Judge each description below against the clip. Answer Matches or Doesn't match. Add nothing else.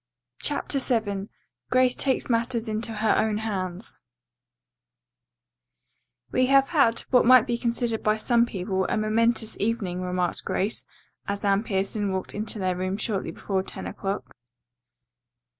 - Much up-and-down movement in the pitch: Doesn't match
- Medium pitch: Doesn't match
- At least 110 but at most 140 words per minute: Matches